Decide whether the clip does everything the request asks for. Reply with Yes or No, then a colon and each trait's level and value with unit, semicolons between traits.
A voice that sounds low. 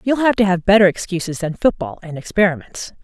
No: high, 190 Hz